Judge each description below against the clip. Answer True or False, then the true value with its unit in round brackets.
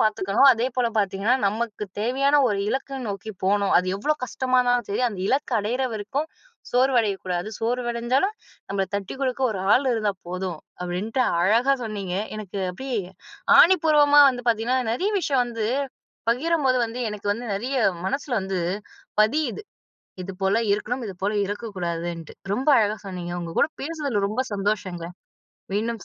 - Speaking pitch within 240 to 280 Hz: False (225 Hz)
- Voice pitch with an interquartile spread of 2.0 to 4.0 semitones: False (4.6 semitones)